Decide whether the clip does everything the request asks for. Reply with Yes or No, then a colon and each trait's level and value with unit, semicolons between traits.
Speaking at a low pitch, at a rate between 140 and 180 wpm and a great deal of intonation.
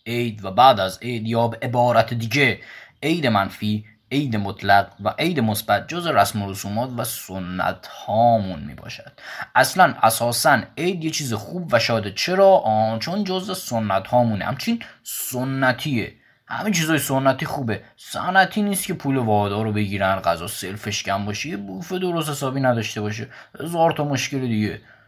Yes: low, 115 Hz; fast, 155 wpm; wide, 5.7 semitones